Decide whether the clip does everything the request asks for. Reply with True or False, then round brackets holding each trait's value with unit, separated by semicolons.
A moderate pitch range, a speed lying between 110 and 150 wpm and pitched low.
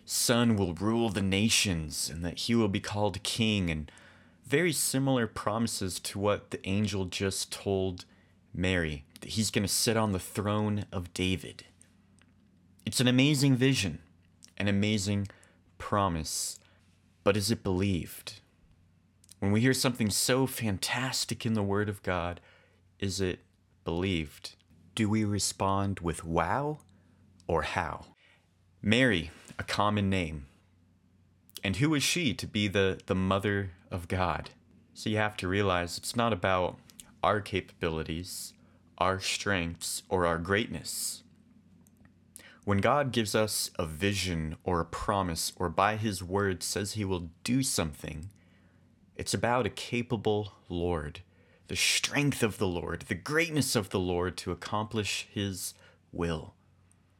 True (3.3 semitones; 140 wpm; 95 Hz)